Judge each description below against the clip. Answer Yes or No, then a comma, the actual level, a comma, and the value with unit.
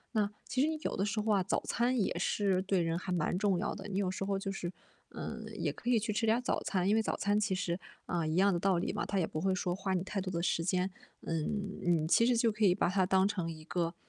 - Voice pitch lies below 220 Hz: Yes, high, 195 Hz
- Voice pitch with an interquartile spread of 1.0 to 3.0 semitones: Yes, narrow, 2.6 semitones